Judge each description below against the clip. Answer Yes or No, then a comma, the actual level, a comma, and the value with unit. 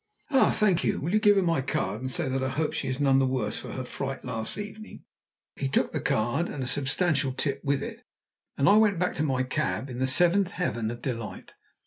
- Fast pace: Yes, fast, 240 wpm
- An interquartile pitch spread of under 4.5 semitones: No, average, 5.3 semitones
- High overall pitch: No, low, 135 Hz